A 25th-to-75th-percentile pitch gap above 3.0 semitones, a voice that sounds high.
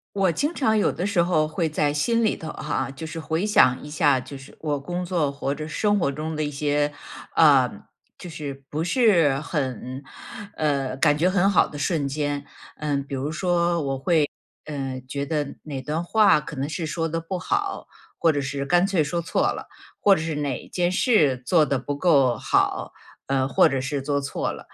No: average, 3.6 semitones; medium, 150 Hz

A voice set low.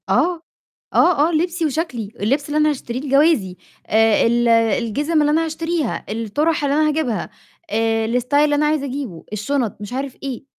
No: very high, 280 Hz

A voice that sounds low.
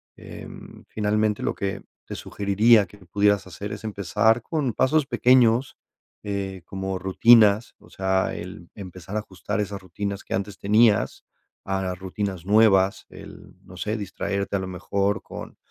Yes: low, 100 Hz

